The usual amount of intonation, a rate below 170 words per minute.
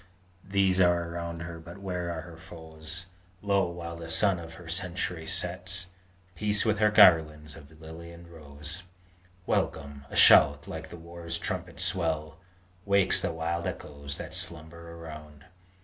No: narrow, 2.0 semitones; average, 150 wpm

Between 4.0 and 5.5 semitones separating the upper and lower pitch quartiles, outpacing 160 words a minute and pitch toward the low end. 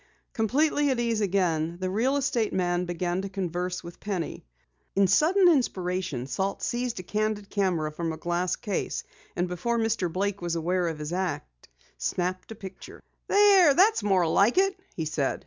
No: average, 4.5 semitones; average, 170 wpm; high, 190 Hz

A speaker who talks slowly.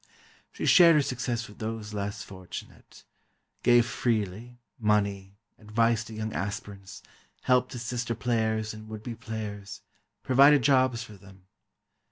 Yes: slow, 125 wpm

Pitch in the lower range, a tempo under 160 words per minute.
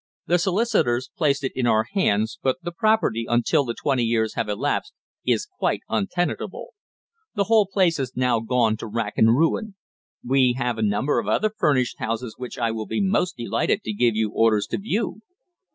No: low, 125 Hz; average, 185 wpm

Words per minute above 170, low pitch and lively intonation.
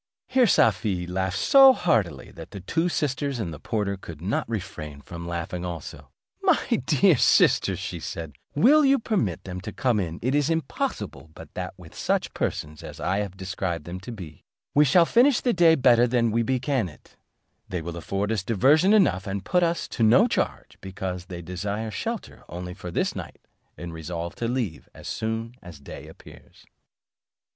Yes: average, 185 wpm; low, 100 Hz; wide, 7.5 semitones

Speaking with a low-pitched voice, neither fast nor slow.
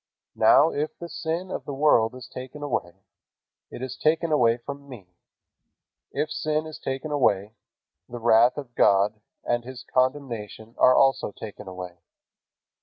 Yes: low, 130 Hz; average, 150 wpm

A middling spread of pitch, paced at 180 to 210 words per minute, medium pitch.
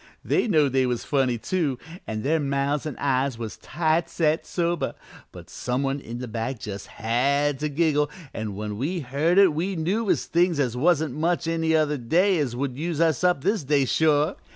Yes: average, 4.5 semitones; average, 195 wpm; medium, 145 Hz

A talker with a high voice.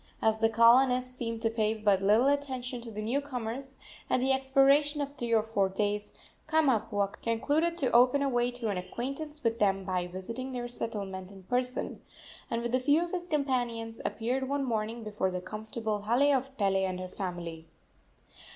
Yes: high, 235 Hz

